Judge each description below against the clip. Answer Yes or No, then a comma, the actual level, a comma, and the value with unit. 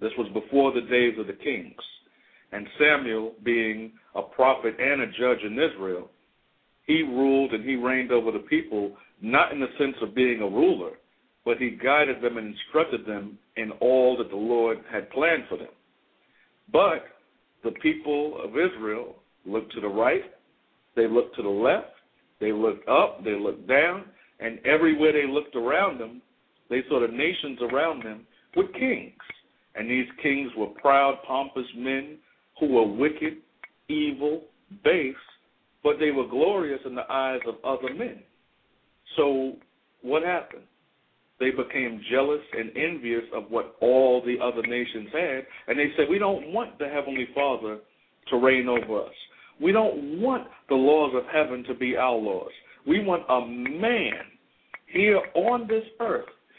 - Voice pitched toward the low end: Yes, low, 130 Hz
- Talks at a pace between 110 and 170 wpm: Yes, average, 160 wpm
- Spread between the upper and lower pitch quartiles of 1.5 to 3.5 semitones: No, average, 4.4 semitones